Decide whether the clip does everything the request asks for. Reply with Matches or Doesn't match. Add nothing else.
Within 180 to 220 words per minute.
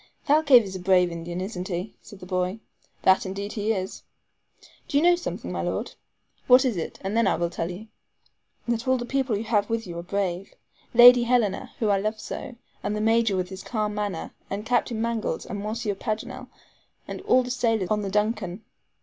Matches